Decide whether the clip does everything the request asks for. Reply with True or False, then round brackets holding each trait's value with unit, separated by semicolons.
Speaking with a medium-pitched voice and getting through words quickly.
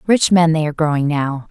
True (160 Hz; 240 wpm)